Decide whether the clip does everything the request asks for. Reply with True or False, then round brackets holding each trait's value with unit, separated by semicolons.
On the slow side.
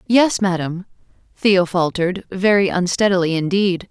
True (105 wpm)